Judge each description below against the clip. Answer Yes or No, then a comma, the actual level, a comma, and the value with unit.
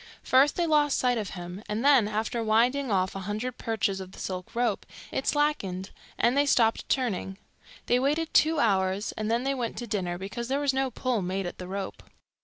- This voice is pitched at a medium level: No, high, 225 Hz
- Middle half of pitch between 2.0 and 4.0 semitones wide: No, wide, 5.4 semitones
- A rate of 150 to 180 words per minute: No, fast, 205 wpm